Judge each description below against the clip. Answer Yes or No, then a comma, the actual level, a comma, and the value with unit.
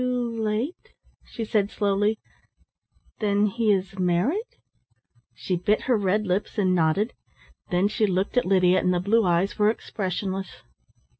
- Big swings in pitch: No, average, 2.8 semitones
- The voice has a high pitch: Yes, high, 200 Hz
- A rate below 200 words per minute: Yes, average, 145 wpm